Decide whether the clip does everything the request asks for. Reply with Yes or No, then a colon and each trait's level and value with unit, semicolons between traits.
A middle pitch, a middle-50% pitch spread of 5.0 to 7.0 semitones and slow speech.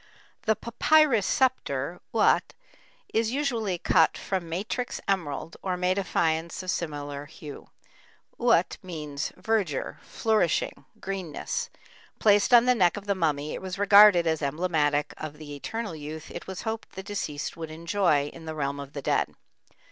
No: medium, 175 Hz; wide, 5.4 semitones; average, 155 wpm